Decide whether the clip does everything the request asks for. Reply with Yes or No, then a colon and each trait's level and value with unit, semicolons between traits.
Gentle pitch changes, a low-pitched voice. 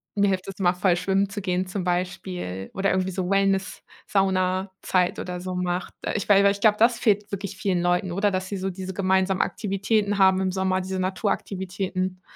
No: narrow, 1.2 semitones; high, 190 Hz